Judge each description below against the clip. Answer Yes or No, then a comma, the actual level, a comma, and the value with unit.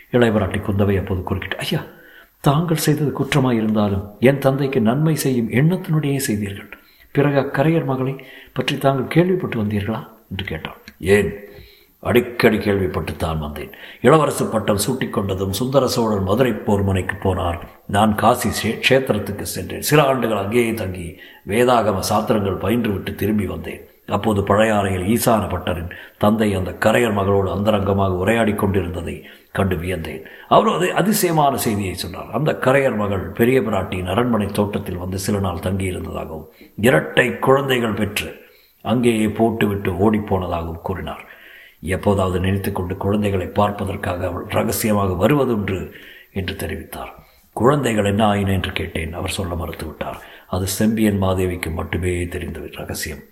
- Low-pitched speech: Yes, low, 100 Hz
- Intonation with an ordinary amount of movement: Yes, average, 3.9 semitones